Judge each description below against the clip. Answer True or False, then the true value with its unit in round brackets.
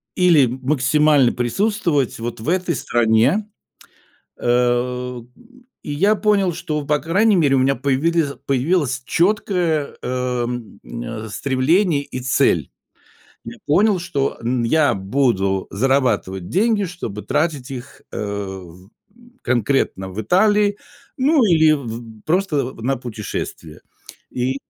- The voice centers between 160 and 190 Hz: False (135 Hz)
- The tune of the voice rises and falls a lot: True (6.0 semitones)